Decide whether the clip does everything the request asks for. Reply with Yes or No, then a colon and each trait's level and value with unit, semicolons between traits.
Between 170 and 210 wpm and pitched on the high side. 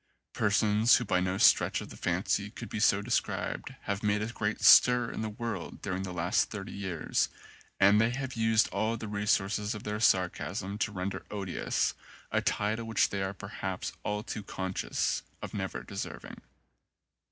No: average, 175 wpm; low, 105 Hz